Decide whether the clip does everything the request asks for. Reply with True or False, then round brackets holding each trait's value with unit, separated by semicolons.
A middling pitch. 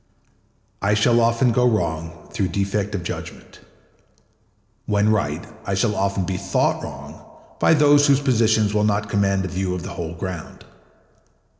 False (100 Hz)